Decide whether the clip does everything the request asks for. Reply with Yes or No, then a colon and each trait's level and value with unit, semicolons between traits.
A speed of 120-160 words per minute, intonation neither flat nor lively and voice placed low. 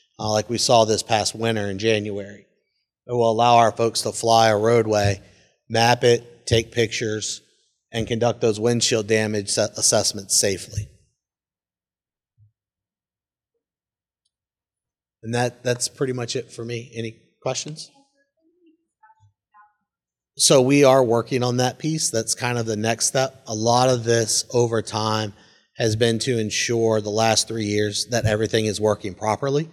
No: average, 145 wpm; narrow, 2.2 semitones; low, 115 Hz